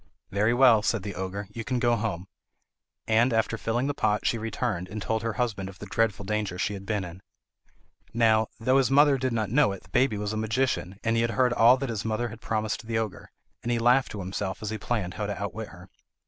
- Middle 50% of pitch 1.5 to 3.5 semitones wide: Yes, average, 2.7 semitones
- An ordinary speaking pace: No, fast, 240 wpm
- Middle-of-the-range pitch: No, low, 110 Hz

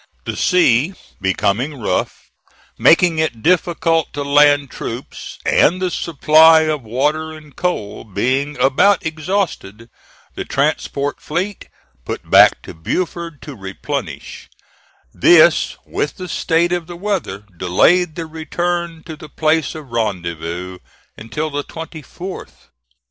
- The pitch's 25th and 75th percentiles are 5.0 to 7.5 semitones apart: Yes, average, 5.3 semitones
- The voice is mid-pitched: Yes, medium, 155 Hz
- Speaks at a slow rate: Yes, slow, 120 wpm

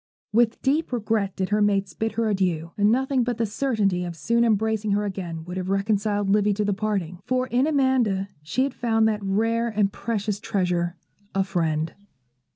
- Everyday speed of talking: Yes, average, 185 wpm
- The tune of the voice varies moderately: Yes, average, 3.1 semitones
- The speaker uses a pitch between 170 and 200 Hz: No, high, 210 Hz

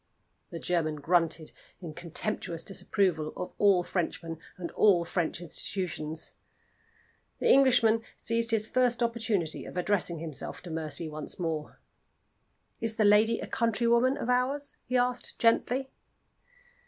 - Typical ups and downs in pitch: No, wide, 5.9 semitones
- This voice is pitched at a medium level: No, high, 195 Hz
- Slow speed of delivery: Yes, slow, 130 wpm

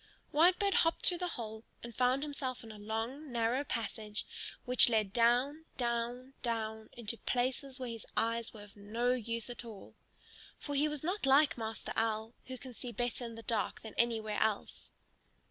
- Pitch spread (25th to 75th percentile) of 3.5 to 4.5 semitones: No, average, 2.9 semitones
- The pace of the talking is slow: No, average, 180 wpm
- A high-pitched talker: Yes, high, 235 Hz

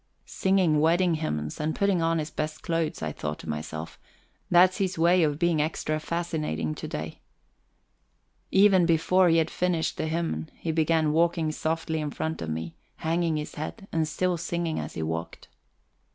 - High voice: No, medium, 160 Hz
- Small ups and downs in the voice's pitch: Yes, narrow, 2.2 semitones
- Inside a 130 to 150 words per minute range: No, average, 170 wpm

